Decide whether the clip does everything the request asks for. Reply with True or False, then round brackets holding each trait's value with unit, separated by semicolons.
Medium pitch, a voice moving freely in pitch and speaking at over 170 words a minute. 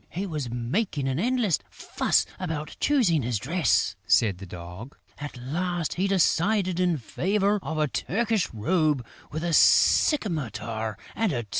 False (160 Hz; 7.5 semitones; 150 wpm)